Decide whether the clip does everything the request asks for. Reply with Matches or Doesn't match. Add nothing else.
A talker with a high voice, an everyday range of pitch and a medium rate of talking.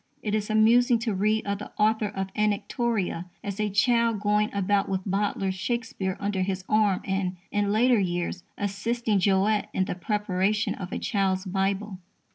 Doesn't match